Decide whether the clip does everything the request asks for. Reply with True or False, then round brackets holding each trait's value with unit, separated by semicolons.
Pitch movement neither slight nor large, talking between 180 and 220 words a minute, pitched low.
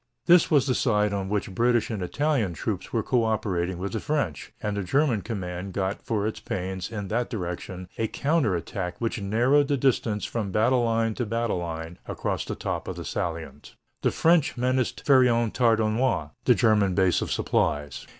True (4.5 semitones; 190 wpm; 110 Hz)